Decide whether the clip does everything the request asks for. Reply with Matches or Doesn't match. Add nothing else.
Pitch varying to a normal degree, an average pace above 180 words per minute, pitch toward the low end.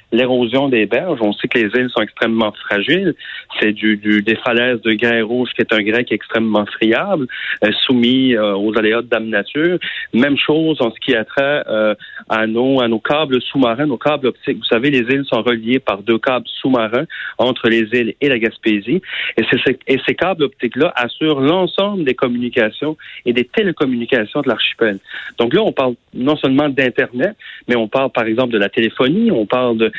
Matches